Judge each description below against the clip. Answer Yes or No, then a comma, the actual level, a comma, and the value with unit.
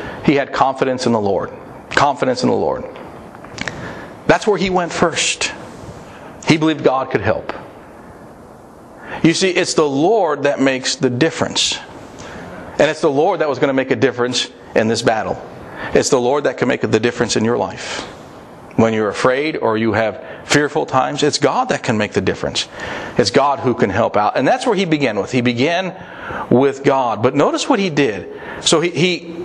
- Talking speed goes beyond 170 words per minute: Yes, average, 190 wpm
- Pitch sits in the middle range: Yes, medium, 145 Hz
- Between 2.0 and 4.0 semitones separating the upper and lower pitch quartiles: No, average, 4.5 semitones